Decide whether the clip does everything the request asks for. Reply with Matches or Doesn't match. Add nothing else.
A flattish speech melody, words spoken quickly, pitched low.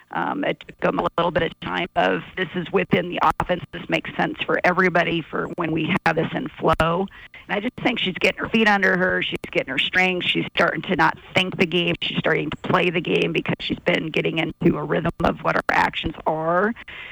Doesn't match